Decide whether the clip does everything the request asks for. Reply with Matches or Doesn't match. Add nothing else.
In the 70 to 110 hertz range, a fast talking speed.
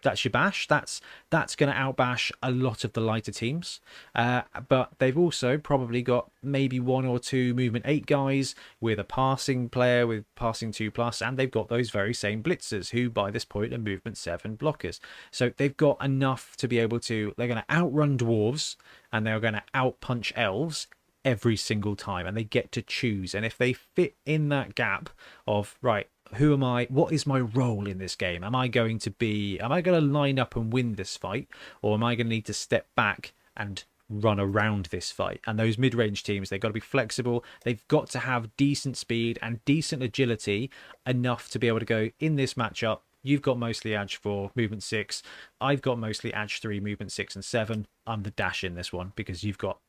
Doesn't match